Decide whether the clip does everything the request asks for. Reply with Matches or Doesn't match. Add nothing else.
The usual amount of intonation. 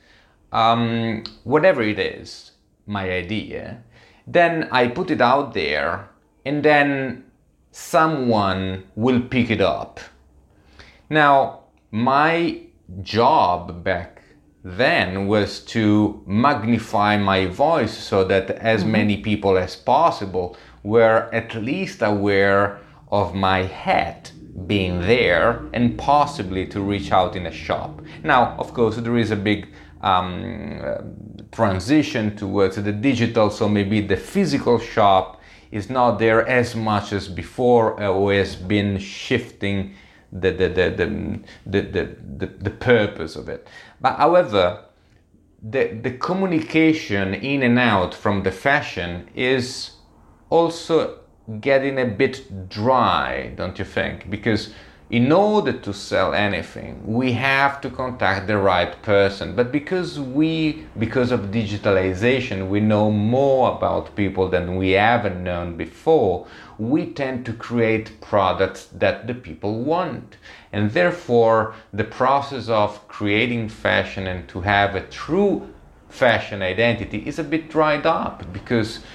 Matches